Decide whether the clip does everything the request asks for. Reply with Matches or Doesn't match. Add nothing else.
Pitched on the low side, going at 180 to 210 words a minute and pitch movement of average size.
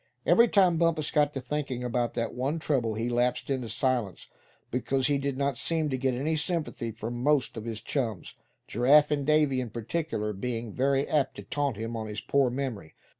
Matches